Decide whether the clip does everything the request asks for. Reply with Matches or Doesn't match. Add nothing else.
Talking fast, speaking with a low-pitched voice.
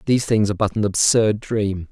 Matches